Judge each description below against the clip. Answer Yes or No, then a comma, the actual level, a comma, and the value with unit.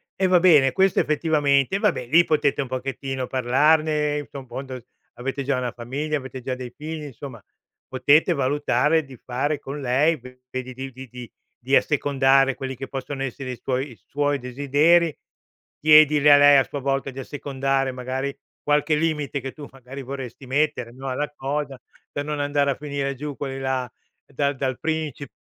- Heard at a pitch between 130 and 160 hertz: Yes, medium, 140 Hz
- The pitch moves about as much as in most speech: No, narrow, 2.1 semitones